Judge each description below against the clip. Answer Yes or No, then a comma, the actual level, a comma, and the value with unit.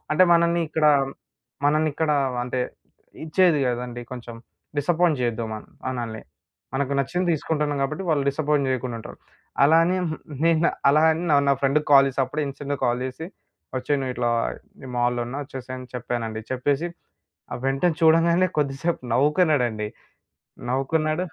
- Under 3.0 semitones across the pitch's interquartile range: No, average, 3.8 semitones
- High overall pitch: No, medium, 140 Hz